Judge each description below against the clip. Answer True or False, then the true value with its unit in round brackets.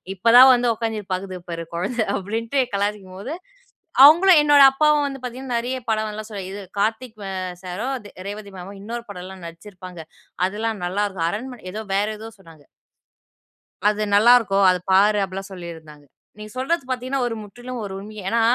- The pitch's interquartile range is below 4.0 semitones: False (4.3 semitones)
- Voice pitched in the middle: False (210 Hz)